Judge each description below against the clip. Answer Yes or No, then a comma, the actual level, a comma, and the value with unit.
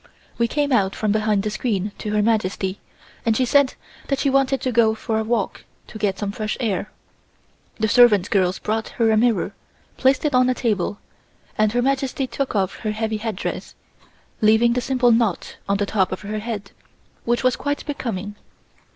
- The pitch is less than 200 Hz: No, high, 220 Hz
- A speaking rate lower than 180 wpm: No, average, 190 wpm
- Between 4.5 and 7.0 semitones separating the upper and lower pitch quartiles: No, average, 3.3 semitones